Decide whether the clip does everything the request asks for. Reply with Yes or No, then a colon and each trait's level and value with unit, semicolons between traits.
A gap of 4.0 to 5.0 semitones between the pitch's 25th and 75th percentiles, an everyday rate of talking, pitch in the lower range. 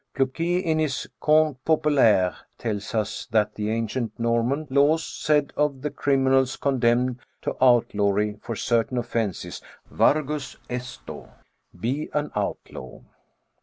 No: average, 4.6 semitones; slow, 120 wpm; low, 130 Hz